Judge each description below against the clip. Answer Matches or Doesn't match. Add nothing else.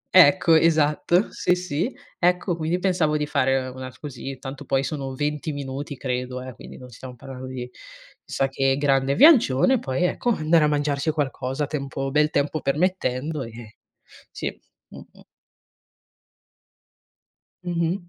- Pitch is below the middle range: Doesn't match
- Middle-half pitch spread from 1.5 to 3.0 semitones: Doesn't match